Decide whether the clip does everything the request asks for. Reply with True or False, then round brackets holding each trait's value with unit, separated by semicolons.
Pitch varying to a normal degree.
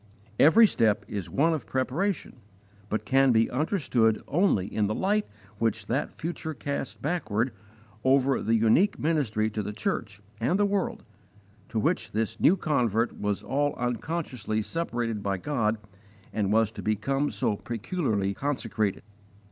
False (5.7 semitones)